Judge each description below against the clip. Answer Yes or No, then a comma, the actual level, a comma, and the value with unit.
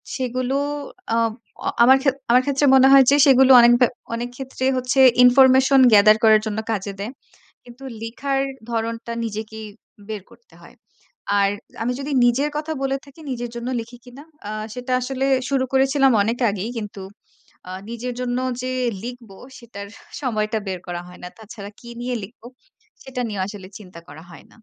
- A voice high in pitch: Yes, high, 240 Hz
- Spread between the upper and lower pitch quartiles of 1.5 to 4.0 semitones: Yes, average, 3.4 semitones